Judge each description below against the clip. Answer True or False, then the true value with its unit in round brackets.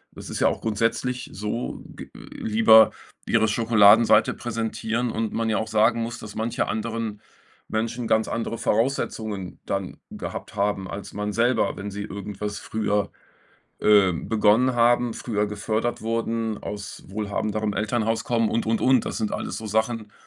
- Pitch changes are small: True (1.7 semitones)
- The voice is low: True (110 Hz)